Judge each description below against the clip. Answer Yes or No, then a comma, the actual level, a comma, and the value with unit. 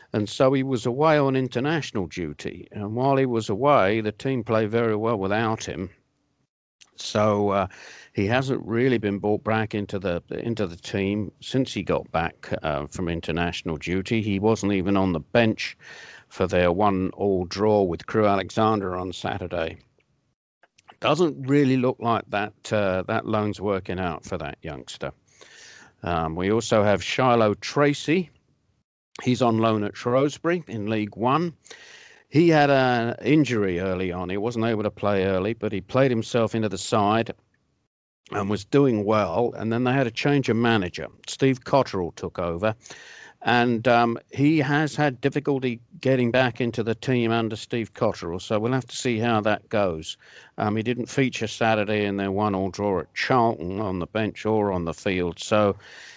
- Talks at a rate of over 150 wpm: Yes, average, 170 wpm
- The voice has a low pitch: Yes, low, 110 Hz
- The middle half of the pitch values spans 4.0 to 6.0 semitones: Yes, average, 4.3 semitones